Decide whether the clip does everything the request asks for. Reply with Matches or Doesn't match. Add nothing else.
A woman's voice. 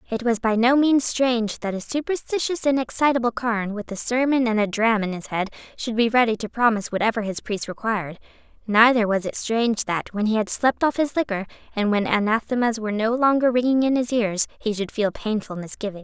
Matches